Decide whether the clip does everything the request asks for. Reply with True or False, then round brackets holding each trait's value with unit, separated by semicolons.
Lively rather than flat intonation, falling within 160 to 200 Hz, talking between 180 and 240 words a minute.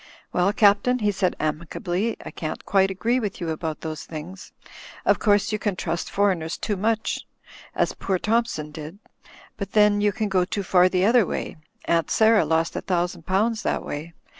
False (3.8 semitones; 190 Hz; 185 wpm)